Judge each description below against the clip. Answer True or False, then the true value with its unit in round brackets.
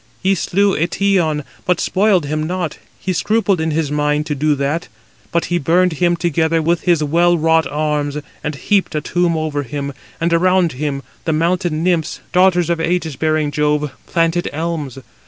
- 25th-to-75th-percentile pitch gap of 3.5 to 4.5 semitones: False (2.8 semitones)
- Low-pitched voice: False (165 Hz)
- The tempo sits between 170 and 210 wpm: True (175 wpm)